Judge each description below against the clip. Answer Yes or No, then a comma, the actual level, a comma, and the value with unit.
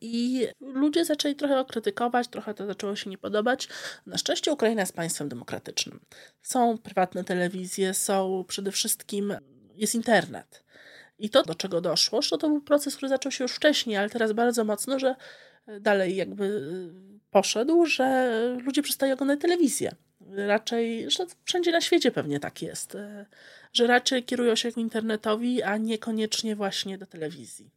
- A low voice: No, high, 220 Hz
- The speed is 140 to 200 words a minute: Yes, average, 155 wpm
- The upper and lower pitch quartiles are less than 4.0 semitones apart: No, average, 4.8 semitones